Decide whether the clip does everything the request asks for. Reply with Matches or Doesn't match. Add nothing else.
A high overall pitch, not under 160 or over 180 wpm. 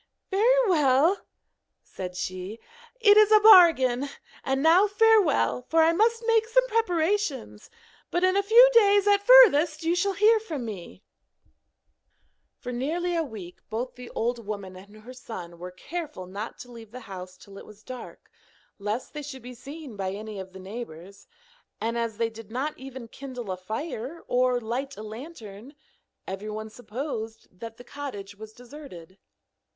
Matches